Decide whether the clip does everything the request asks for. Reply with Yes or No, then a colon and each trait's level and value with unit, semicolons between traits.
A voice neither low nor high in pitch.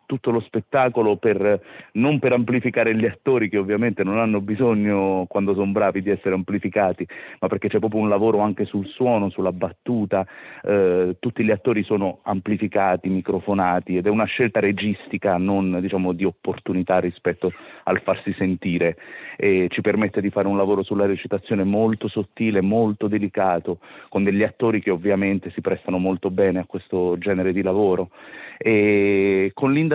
No: low, 100 Hz